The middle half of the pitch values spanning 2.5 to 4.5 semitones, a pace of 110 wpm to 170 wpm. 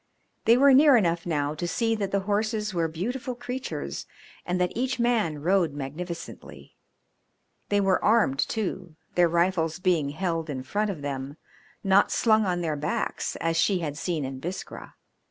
No: average, 5.1 semitones; average, 165 wpm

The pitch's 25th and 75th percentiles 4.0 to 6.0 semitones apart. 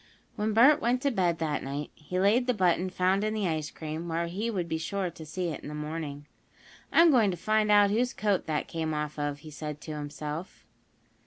Yes: wide, 5.5 semitones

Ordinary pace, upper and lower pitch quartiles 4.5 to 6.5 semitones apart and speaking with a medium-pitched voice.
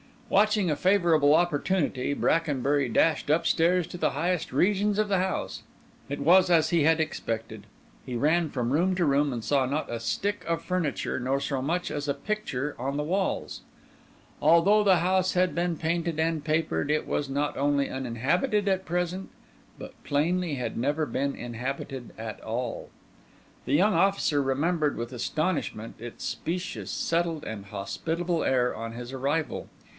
Yes: average, 160 wpm; average, 4.9 semitones; medium, 155 Hz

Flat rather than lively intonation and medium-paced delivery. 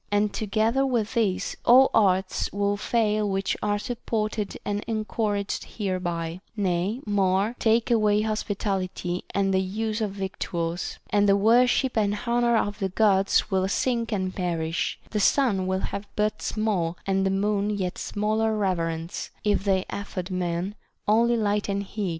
Yes: narrow, 2.3 semitones; average, 155 wpm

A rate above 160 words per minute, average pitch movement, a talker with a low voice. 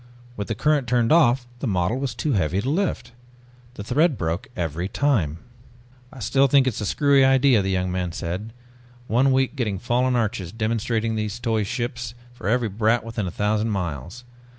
Yes: average, 180 wpm; average, 4.4 semitones; low, 115 Hz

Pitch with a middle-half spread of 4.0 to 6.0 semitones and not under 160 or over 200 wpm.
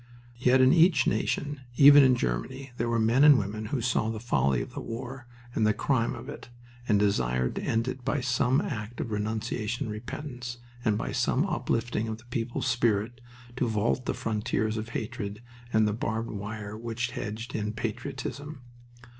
No: average, 2.8 semitones; average, 180 wpm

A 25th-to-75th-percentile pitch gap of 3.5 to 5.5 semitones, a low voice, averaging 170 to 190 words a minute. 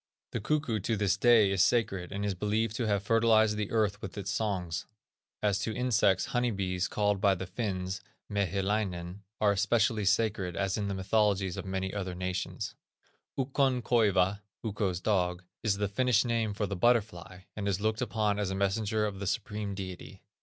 No: narrow, 2.5 semitones; low, 100 Hz; average, 180 wpm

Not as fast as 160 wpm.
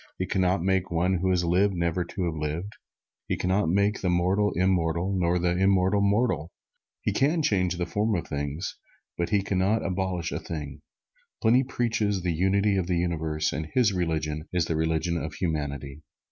No: average, 190 wpm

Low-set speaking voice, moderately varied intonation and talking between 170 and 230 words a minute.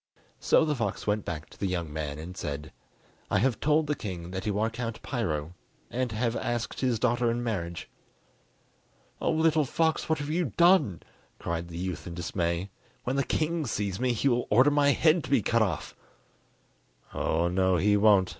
No: low, 110 Hz; wide, 7.3 semitones; average, 190 wpm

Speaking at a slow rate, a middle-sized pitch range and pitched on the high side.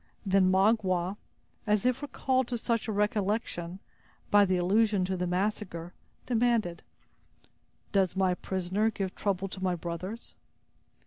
Yes: slow, 130 wpm; average, 3.0 semitones; high, 195 Hz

